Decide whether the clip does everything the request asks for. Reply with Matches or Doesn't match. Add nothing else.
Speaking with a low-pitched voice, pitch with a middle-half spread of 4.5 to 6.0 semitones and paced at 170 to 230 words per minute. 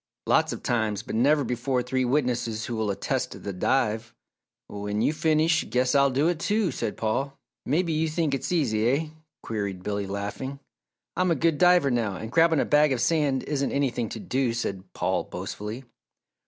Matches